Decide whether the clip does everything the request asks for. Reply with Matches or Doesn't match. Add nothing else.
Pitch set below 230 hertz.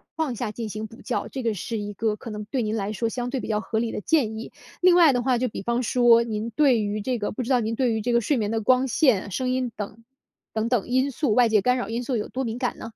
Doesn't match